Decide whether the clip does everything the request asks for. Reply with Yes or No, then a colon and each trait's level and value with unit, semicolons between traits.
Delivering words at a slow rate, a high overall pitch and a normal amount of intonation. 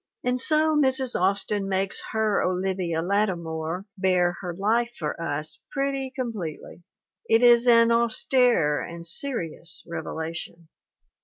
No: slow, 120 wpm; high, 195 Hz; wide, 6.0 semitones